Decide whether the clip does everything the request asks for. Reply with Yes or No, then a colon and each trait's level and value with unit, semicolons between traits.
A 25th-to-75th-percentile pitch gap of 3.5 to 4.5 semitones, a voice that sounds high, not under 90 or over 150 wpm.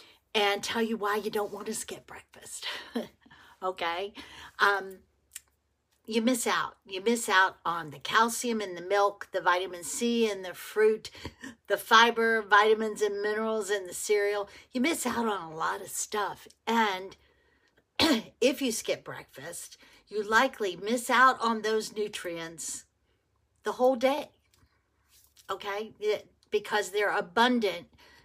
No: average, 3.0 semitones; high, 215 Hz; average, 140 wpm